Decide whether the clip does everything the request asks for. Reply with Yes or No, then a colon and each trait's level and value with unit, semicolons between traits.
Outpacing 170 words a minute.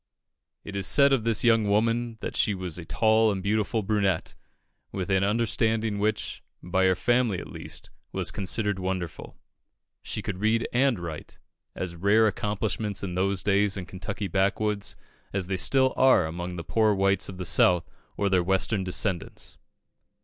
No: average, 165 wpm